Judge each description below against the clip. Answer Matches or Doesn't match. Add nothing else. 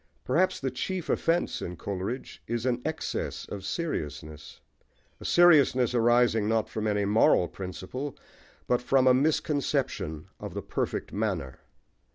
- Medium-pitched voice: Doesn't match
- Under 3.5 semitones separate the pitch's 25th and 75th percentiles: Doesn't match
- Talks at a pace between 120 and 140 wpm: Matches